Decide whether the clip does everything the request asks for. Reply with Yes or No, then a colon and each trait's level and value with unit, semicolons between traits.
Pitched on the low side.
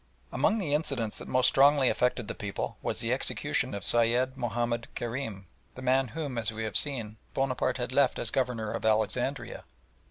Yes: low, 125 Hz